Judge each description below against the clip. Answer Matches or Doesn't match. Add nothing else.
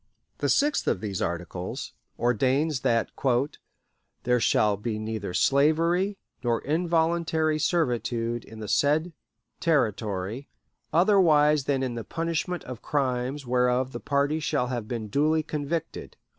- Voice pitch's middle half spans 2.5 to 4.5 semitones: Doesn't match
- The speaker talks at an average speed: Doesn't match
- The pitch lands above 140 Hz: Doesn't match